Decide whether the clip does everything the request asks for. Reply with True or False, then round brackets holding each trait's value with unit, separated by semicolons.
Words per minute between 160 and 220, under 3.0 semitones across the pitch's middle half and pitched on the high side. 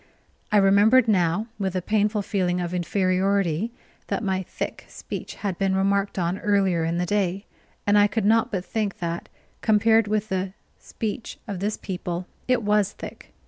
True (170 wpm; 2.4 semitones; 195 Hz)